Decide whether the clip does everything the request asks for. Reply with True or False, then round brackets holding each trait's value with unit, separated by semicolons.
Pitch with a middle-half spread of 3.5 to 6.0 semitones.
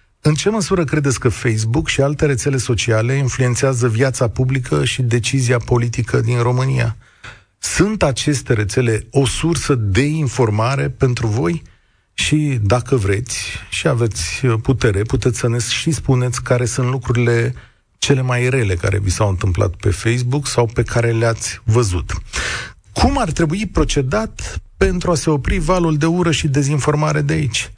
True (4.1 semitones)